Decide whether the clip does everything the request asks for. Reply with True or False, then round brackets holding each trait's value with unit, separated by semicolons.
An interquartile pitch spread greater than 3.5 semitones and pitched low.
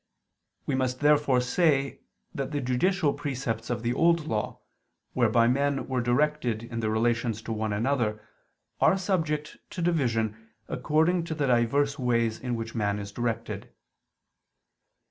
True (4.3 semitones; 125 Hz)